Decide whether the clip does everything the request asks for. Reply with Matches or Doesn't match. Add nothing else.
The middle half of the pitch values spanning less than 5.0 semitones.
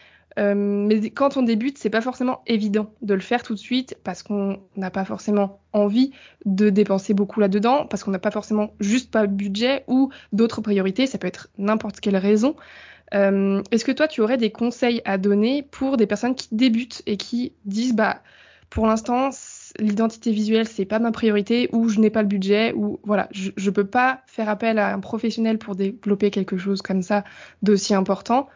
Matches